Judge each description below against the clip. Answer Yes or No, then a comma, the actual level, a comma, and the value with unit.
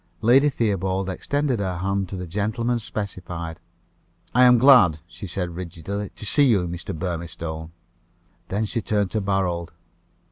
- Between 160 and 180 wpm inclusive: No, average, 140 wpm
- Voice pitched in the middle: No, very low, 95 Hz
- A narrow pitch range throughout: No, average, 4.2 semitones